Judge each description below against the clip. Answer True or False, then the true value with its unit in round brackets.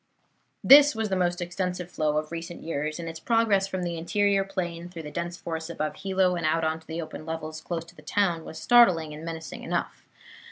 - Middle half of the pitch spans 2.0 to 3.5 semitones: True (2.6 semitones)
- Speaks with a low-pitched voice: False (170 Hz)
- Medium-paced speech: False (215 wpm)